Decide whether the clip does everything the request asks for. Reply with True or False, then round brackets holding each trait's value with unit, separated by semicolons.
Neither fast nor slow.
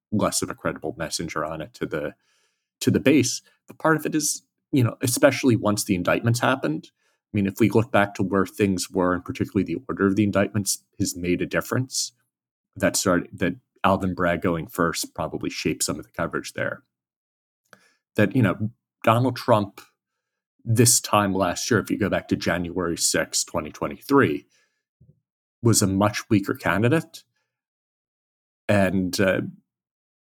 True (165 wpm)